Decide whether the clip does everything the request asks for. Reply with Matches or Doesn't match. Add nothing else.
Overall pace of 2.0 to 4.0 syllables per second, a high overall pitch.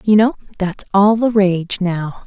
Matches